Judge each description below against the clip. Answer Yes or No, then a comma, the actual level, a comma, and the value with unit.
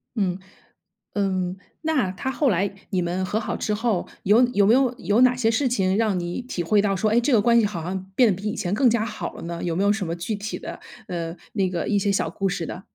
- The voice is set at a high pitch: Yes, high, 205 Hz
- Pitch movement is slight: No, average, 3.7 semitones